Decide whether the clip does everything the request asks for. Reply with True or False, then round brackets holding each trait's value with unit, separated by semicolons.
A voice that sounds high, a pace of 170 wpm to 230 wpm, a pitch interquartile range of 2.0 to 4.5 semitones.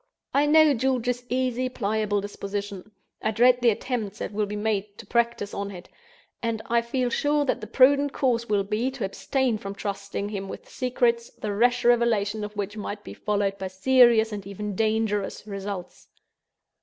True (220 Hz; 175 wpm; 3.3 semitones)